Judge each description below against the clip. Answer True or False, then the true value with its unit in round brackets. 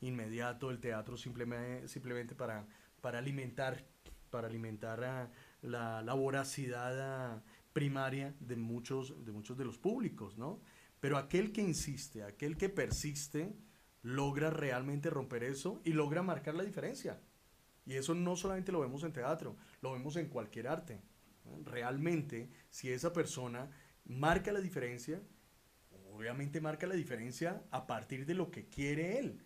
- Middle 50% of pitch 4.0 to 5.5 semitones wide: True (4.6 semitones)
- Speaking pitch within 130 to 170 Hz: True (135 Hz)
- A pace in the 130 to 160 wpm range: True (140 wpm)